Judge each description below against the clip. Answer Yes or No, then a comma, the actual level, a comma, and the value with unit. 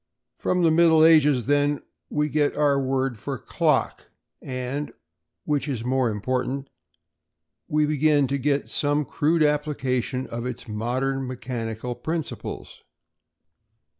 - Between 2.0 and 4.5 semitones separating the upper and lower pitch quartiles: Yes, average, 2.8 semitones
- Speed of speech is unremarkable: No, slow, 120 wpm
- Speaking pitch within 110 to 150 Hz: Yes, medium, 140 Hz